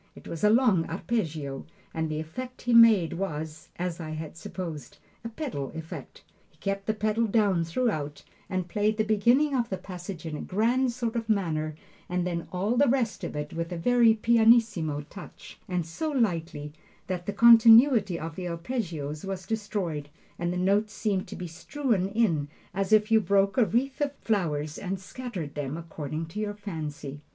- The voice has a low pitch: No, high, 190 Hz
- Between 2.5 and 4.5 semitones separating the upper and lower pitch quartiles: No, wide, 5.5 semitones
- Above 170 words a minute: Yes, average, 185 wpm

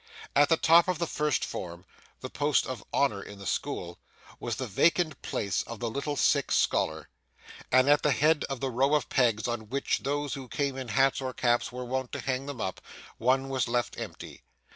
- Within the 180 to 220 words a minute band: Yes, fast, 205 wpm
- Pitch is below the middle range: Yes, low, 130 Hz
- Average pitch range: Yes, average, 3.3 semitones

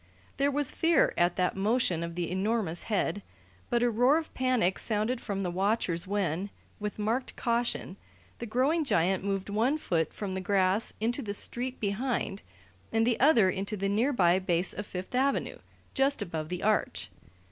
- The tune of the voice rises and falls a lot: No, average, 4.5 semitones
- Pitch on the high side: Yes, high, 210 Hz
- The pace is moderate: Yes, average, 170 wpm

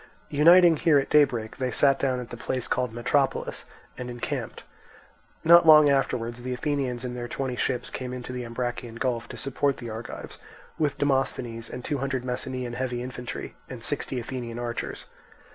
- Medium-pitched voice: No, low, 125 Hz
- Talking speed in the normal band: Yes, average, 170 wpm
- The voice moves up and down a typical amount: No, narrow, 2.2 semitones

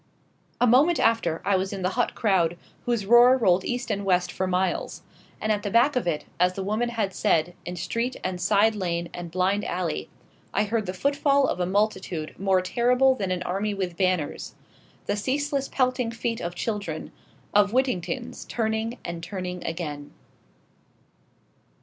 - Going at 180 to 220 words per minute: No, average, 170 wpm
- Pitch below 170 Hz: No, high, 200 Hz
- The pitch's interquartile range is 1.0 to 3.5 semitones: No, average, 4.7 semitones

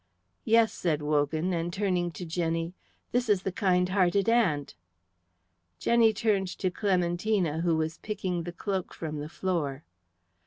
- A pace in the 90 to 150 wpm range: Yes, average, 145 wpm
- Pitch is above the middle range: No, medium, 180 Hz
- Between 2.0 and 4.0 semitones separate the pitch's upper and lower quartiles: Yes, average, 3.4 semitones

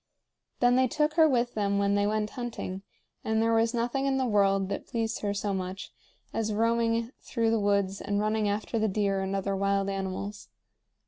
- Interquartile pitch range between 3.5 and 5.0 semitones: No, narrow, 2.6 semitones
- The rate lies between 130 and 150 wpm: No, average, 195 wpm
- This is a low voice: No, high, 210 Hz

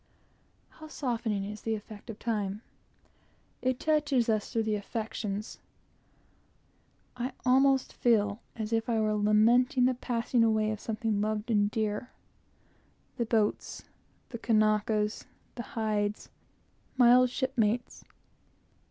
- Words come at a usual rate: No, slow, 120 wpm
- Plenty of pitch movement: No, narrow, 2.5 semitones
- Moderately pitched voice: No, high, 225 Hz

